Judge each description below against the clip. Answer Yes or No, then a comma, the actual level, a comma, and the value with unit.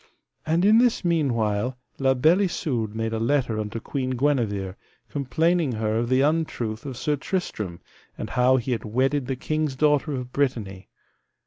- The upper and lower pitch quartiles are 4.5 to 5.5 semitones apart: Yes, average, 4.8 semitones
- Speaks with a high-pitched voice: No, low, 130 Hz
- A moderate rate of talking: Yes, average, 160 wpm